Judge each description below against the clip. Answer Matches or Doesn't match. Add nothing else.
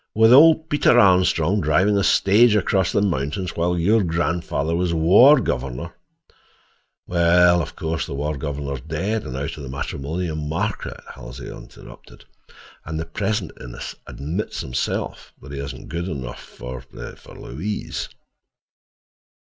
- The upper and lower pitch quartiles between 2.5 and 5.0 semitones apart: Doesn't match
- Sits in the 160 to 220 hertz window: Doesn't match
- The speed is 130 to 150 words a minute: Matches